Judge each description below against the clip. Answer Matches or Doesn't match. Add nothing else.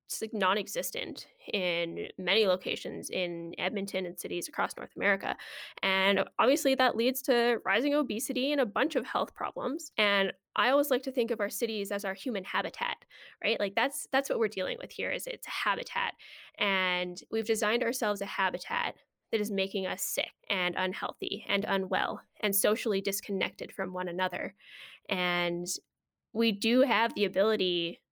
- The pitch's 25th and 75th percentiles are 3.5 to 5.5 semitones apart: Matches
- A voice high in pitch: Matches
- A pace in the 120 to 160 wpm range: Doesn't match